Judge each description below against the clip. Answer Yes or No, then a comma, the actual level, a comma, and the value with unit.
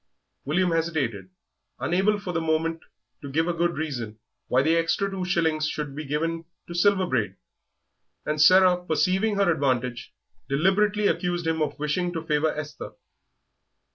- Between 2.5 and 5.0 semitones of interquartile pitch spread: Yes, average, 3.3 semitones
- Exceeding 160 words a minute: No, average, 150 wpm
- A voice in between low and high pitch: Yes, medium, 165 Hz